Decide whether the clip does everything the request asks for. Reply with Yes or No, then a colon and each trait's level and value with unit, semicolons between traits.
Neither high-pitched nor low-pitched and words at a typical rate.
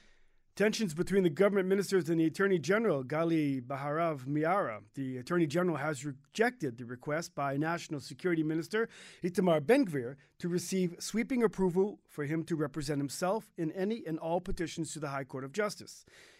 Yes: medium, 170 Hz; average, 165 wpm